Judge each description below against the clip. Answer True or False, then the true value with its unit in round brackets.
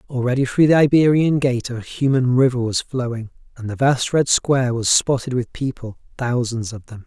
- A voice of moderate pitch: False (125 Hz)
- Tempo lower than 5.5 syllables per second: True (5.1 syllables/s)